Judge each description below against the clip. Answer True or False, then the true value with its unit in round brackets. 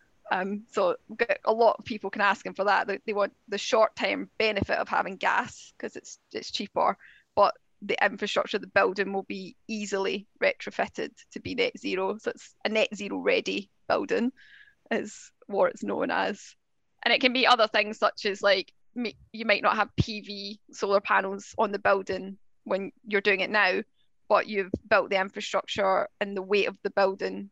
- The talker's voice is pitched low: False (205 Hz)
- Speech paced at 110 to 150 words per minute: False (185 wpm)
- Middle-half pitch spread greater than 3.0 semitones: False (2.5 semitones)